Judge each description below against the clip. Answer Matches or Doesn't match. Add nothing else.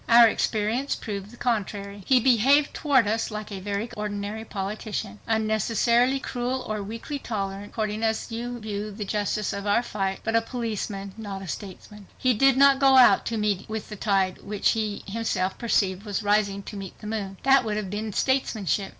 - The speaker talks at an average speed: Matches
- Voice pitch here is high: Matches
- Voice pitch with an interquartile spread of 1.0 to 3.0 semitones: Matches